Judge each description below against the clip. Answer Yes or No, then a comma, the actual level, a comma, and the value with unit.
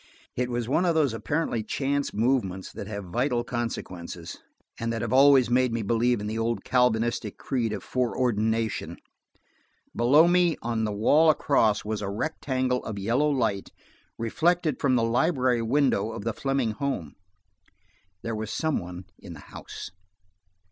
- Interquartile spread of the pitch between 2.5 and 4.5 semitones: Yes, average, 3.7 semitones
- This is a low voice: Yes, low, 120 Hz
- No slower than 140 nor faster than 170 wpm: Yes, average, 155 wpm